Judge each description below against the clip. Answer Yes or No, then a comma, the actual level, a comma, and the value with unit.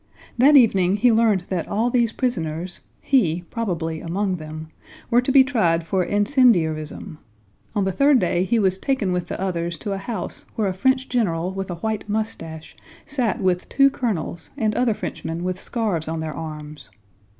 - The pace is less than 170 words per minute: No, average, 175 wpm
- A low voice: No, high, 190 Hz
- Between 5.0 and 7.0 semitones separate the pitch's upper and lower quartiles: Yes, wide, 5.6 semitones